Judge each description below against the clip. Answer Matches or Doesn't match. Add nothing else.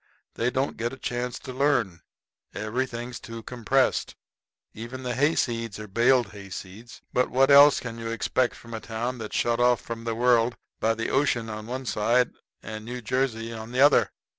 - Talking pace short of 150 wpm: Doesn't match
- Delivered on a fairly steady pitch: Matches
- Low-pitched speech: Matches